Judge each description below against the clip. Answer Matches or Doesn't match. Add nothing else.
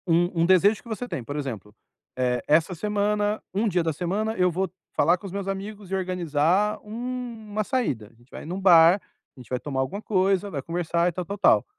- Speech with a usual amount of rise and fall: Matches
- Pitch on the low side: Doesn't match